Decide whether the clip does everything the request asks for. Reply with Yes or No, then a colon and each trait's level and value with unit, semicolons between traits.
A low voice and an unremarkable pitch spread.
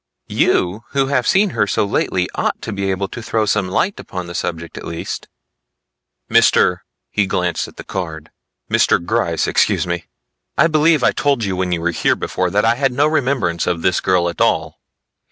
No: very low, 95 Hz; wide, 6.3 semitones